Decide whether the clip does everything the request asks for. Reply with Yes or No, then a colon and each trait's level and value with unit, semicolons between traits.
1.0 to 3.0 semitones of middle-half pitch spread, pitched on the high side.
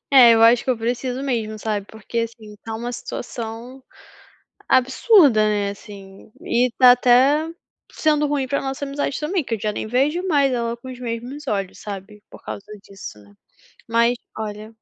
No: average, 3.6 semitones; high, 240 Hz